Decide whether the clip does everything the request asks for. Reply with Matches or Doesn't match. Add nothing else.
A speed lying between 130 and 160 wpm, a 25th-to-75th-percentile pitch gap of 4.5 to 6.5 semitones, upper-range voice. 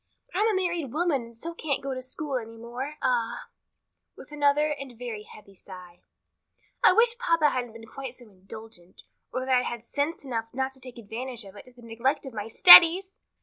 Doesn't match